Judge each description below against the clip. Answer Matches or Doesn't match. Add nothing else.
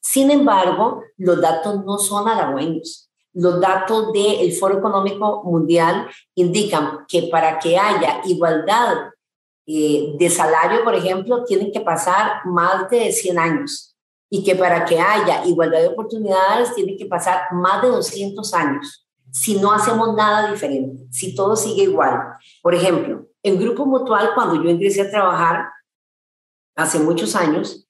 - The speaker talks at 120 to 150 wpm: Matches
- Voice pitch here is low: Doesn't match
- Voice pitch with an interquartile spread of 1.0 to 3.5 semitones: Doesn't match